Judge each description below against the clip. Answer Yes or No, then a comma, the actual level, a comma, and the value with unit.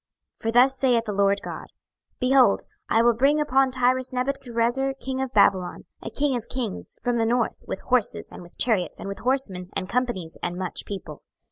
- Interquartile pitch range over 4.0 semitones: Yes, average, 4.5 semitones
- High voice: Yes, high, 240 Hz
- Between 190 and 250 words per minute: Yes, average, 195 wpm